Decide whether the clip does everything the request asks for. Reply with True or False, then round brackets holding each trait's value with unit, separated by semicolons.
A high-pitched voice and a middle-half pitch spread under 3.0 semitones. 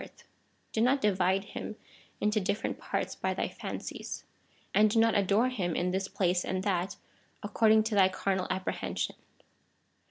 True (200 Hz; 2.6 semitones)